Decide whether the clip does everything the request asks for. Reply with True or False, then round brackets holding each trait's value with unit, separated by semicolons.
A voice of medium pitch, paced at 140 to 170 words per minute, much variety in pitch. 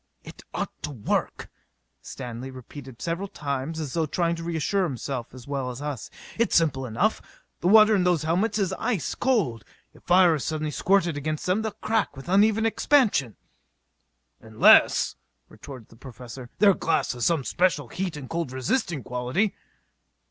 True (155 Hz; 165 wpm; 6.5 semitones)